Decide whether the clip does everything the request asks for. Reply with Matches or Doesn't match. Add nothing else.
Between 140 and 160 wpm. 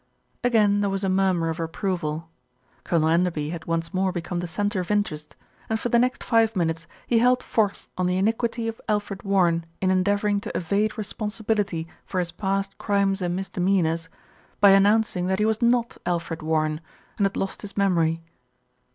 Doesn't match